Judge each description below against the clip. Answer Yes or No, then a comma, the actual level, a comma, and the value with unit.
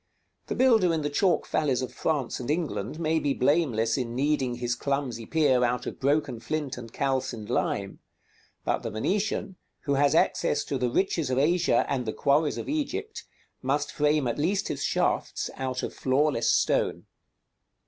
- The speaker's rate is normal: Yes, average, 170 wpm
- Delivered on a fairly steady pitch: No, average, 4.1 semitones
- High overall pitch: No, medium, 140 Hz